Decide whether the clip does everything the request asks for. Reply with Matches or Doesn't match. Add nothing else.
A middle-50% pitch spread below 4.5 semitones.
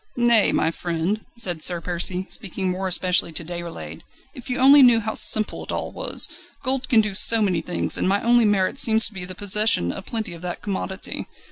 Matches